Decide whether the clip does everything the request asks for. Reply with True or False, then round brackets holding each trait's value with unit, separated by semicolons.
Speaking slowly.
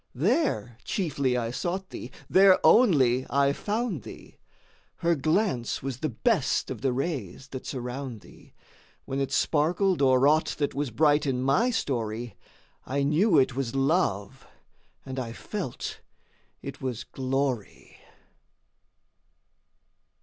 True (130 wpm)